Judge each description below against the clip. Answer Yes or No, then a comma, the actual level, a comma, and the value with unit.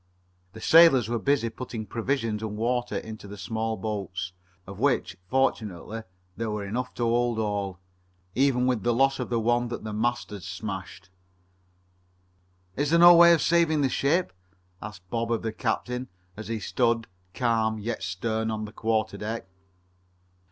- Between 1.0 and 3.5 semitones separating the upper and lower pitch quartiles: Yes, average, 2.8 semitones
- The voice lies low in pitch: Yes, low, 115 Hz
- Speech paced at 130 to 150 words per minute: No, average, 160 wpm